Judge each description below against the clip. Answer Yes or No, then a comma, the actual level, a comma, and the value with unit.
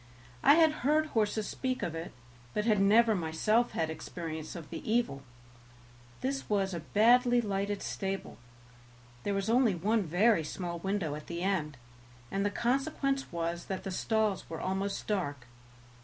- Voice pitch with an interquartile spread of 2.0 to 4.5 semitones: No, wide, 5.4 semitones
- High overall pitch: Yes, high, 200 Hz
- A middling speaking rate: Yes, average, 155 wpm